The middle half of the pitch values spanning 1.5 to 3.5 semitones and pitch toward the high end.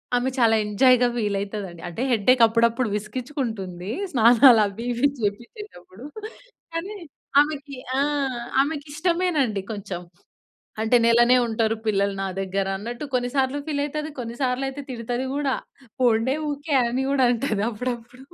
No: average, 4.2 semitones; high, 240 Hz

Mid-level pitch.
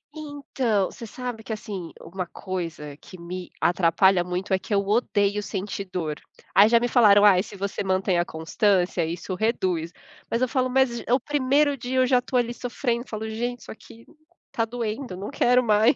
No: high, 210 Hz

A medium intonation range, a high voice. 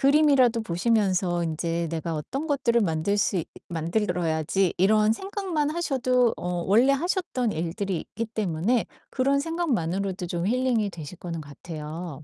No: wide, 7.0 semitones; high, 200 Hz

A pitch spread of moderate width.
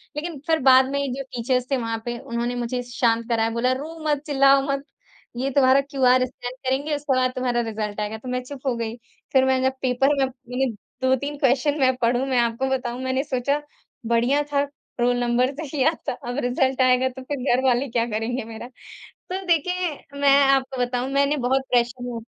No: narrow, 2.2 semitones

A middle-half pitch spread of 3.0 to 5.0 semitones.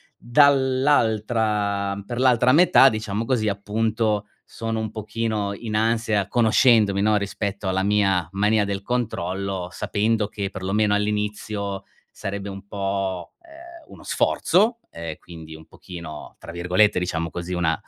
No: narrow, 2.5 semitones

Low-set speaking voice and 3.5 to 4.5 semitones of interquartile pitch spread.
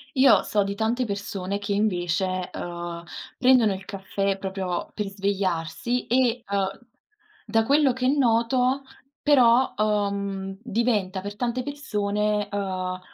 No: high, 205 Hz; average, 3.9 semitones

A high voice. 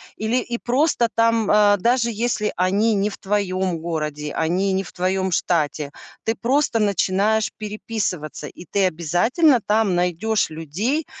Yes: high, 200 Hz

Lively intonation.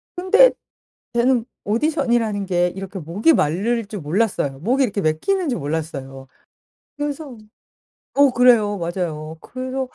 Yes: wide, 7.5 semitones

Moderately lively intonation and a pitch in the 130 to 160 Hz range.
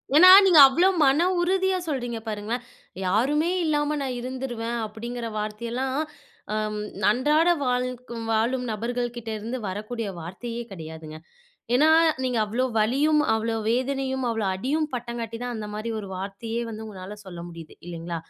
No: average, 3.6 semitones; high, 235 Hz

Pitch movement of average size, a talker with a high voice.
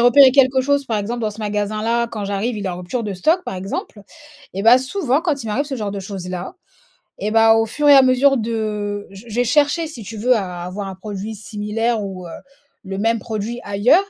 Yes: average, 3.8 semitones; high, 220 Hz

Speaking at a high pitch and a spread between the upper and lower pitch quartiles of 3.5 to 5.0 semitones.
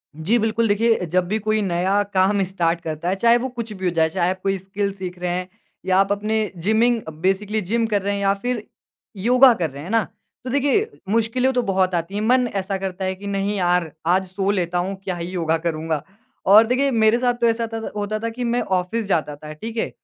Yes: high, 200 Hz; average, 3.9 semitones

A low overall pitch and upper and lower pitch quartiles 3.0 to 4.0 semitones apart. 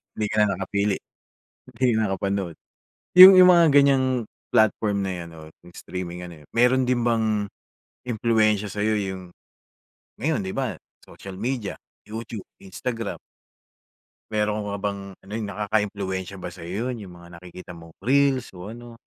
Yes: low, 105 Hz; average, 3.6 semitones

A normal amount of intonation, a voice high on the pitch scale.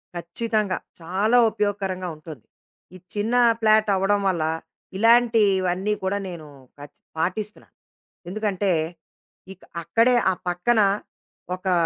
Yes: average, 3.1 semitones; high, 195 Hz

